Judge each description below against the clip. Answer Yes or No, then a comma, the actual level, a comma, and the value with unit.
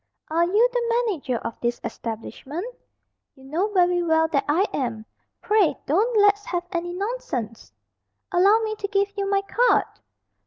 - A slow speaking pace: No, average, 155 wpm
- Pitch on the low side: No, very high, 360 Hz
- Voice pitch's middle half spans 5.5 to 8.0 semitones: Yes, wide, 5.8 semitones